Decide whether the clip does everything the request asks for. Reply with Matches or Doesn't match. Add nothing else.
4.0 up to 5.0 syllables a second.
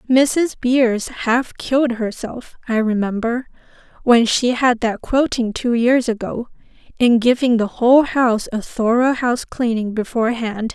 Matches